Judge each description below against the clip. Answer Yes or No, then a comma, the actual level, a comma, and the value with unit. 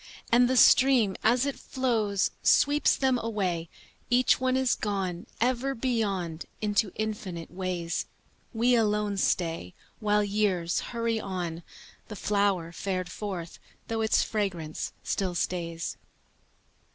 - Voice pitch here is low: No, high, 205 Hz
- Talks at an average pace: No, slow, 120 wpm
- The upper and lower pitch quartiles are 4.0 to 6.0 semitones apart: Yes, average, 4.5 semitones